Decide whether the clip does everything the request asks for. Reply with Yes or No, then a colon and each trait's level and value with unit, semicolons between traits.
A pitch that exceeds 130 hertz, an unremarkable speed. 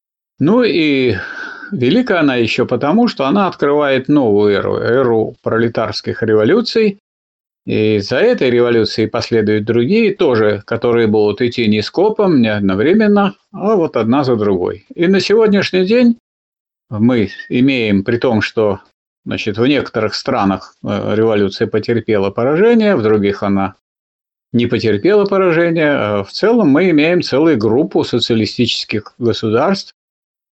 No: low, 120 Hz; average, 130 wpm